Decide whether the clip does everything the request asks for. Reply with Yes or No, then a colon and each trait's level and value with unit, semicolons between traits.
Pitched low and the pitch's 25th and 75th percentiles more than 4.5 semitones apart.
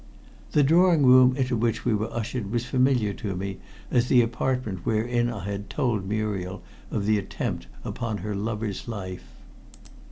No: low, 110 Hz; average, 3.7 semitones